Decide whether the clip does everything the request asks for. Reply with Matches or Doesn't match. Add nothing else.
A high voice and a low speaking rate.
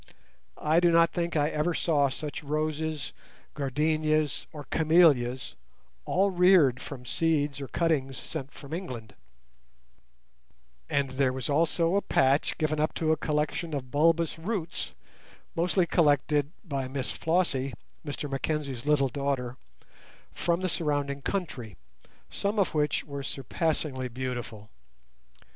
Doesn't match